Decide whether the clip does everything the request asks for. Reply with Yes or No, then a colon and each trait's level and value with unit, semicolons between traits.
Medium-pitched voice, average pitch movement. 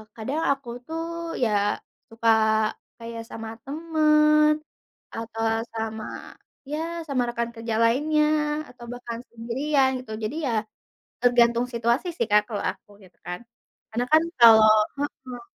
No: high, 240 Hz; average, 4.2 semitones